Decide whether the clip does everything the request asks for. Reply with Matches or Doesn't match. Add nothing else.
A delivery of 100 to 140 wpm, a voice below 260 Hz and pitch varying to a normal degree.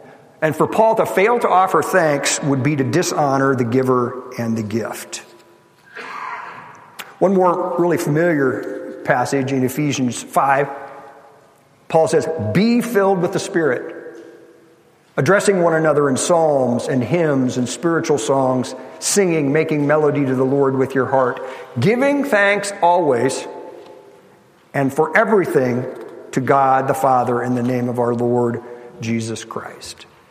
Matches